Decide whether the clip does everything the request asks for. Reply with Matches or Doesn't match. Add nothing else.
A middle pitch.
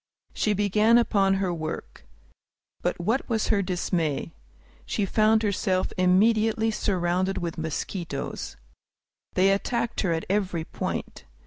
Doesn't match